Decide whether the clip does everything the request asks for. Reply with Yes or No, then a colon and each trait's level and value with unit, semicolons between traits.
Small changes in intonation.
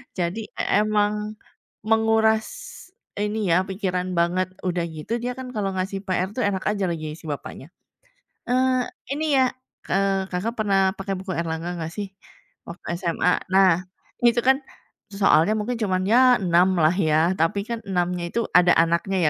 No: average, 3.5 semitones